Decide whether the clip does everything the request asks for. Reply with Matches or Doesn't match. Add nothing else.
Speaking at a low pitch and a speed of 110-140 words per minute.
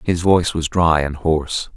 Doesn't match